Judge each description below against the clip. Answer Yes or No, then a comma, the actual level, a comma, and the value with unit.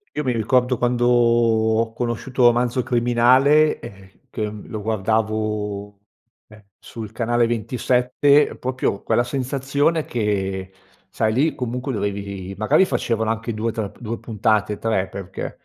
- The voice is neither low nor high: No, low, 115 Hz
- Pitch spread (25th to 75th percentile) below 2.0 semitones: No, average, 2.7 semitones